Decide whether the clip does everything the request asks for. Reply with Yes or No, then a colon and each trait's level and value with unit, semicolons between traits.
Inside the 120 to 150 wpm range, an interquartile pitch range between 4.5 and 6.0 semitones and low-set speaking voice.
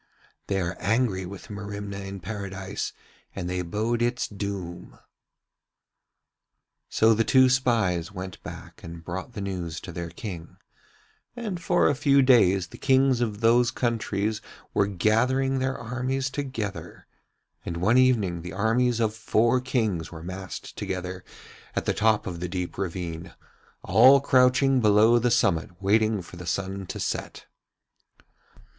Yes: average, 145 wpm; average, 4.9 semitones; low, 105 Hz